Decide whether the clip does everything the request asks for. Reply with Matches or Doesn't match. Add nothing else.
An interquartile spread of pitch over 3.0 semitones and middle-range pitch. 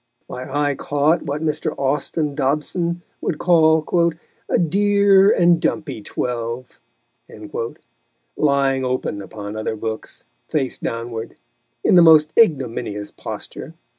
Matches